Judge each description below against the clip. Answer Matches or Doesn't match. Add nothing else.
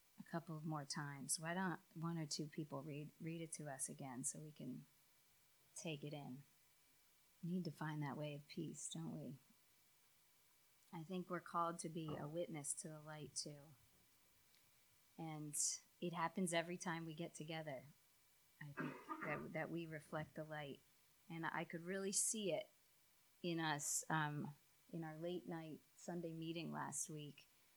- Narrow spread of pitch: Matches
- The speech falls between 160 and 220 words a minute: Matches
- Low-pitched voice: Doesn't match